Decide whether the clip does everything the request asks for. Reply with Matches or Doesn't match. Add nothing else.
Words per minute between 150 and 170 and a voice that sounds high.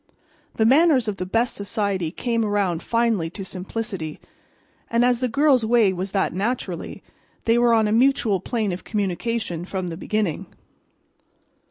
Matches